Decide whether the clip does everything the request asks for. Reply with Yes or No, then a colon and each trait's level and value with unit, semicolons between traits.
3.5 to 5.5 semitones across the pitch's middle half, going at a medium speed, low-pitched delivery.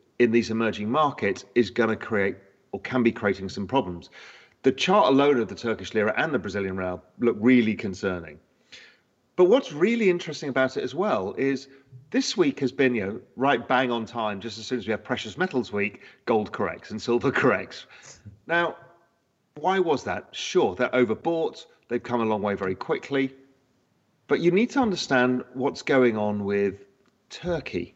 Yes: average, 4.3 semitones; average, 180 wpm; low, 120 Hz